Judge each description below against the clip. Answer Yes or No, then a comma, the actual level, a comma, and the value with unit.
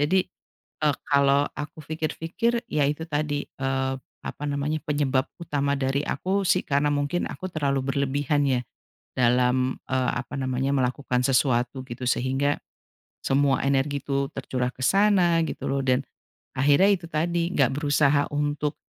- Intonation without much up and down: Yes, narrow, 2.2 semitones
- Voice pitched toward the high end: No, medium, 140 Hz